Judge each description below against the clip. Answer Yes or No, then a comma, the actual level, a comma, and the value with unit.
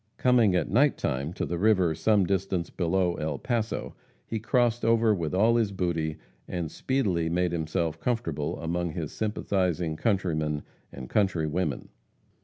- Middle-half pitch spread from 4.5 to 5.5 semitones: Yes, average, 5.1 semitones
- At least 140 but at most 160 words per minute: Yes, average, 145 wpm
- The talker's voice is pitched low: Yes, very low, 90 Hz